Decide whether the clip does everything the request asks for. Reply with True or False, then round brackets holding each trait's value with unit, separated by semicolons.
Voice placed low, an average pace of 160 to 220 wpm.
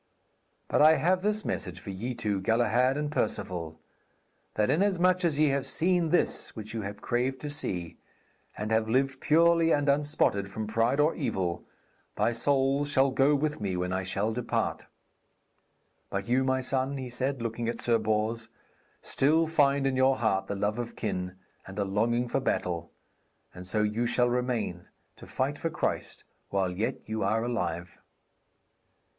True (120 Hz; 165 wpm)